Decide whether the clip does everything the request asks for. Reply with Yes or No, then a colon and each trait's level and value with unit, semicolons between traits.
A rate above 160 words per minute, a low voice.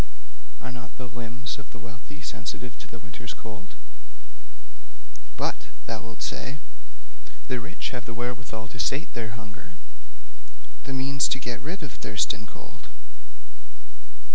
No: average, 140 wpm; low, 120 Hz